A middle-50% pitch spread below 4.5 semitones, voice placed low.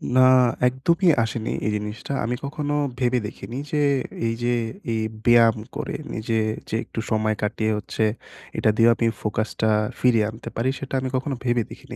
Yes: average, 2.8 semitones; low, 115 Hz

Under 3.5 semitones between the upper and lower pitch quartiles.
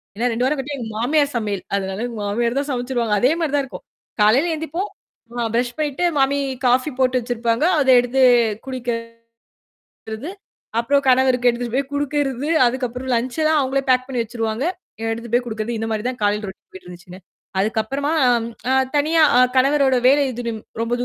Yes: average, 3.1 semitones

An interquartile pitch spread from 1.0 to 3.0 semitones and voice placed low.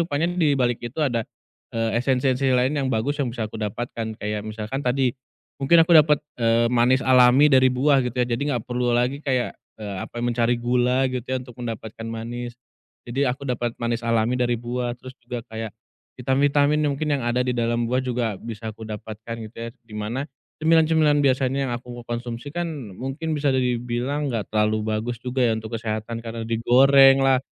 Yes: narrow, 2.5 semitones; low, 125 Hz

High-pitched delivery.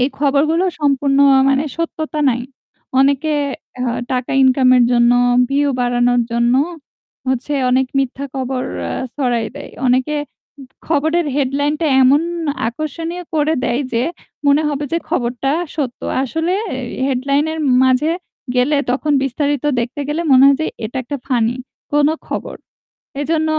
Yes: very high, 275 Hz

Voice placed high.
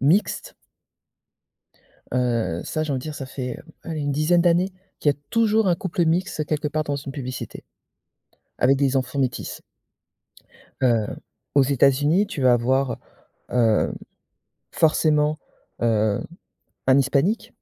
No: medium, 140 Hz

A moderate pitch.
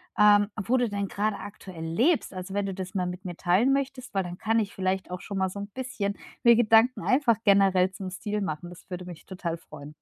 No: high, 195 Hz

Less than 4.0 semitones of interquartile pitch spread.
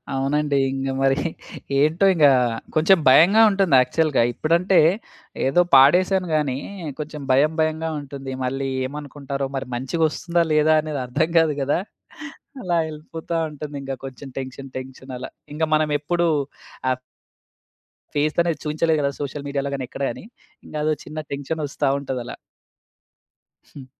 Yes: average, 2.8 semitones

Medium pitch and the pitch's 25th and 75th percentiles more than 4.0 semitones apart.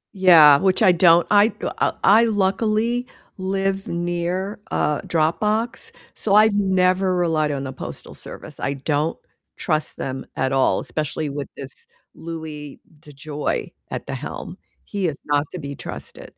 Yes: medium, 170 Hz; average, 4.8 semitones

